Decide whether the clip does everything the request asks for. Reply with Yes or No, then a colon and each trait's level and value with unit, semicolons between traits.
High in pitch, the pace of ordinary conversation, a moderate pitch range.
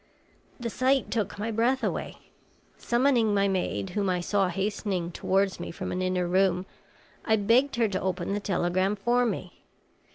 Yes: high, 200 Hz; average, 165 wpm; average, 3.8 semitones